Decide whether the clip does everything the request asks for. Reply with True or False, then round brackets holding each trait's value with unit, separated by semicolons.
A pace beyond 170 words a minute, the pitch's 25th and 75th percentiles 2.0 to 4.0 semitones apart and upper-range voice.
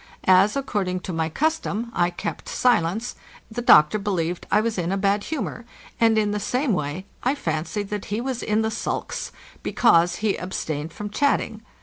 False (180 wpm; 4.4 semitones; 205 Hz)